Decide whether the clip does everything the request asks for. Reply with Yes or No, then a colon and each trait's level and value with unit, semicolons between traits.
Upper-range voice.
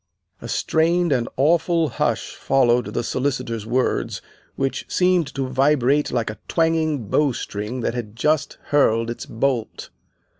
No: low, 135 Hz